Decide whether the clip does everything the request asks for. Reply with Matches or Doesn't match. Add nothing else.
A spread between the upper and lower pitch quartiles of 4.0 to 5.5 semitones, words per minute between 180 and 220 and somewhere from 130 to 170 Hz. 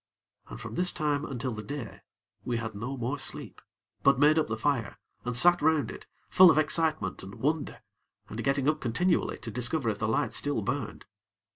Matches